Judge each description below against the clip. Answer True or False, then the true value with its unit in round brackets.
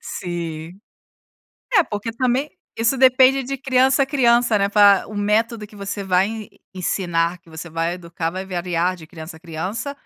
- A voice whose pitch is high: True (200 Hz)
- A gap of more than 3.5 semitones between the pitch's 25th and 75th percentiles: True (5.5 semitones)